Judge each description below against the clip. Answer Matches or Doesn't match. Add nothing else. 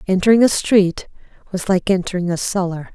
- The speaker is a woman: Matches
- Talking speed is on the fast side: Doesn't match